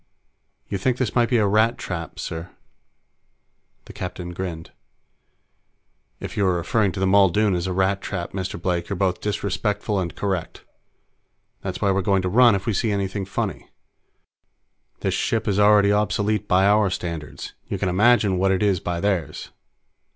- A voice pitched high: No, low, 100 Hz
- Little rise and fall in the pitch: Yes, narrow, 2.2 semitones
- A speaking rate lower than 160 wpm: No, average, 170 wpm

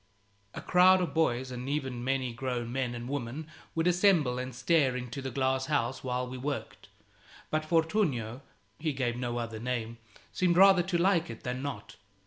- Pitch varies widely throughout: No, average, 4.7 semitones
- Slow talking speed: No, average, 175 wpm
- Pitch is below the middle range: Yes, low, 130 Hz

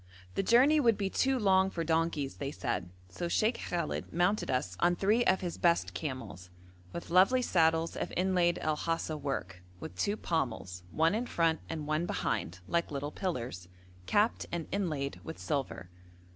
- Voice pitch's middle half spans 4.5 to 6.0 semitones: Yes, average, 5.1 semitones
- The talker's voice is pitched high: No, medium, 165 Hz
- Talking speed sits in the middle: Yes, average, 170 wpm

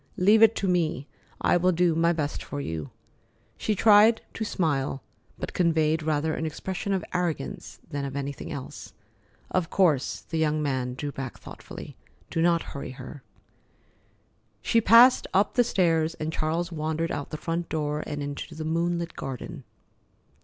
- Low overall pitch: No, medium, 160 Hz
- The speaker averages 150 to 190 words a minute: Yes, average, 160 wpm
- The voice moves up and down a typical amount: Yes, average, 3.5 semitones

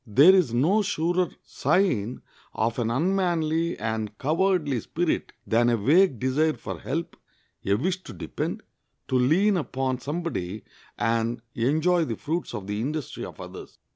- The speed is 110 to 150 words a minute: Yes, average, 145 wpm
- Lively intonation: Yes, wide, 7.0 semitones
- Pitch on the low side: No, medium, 145 Hz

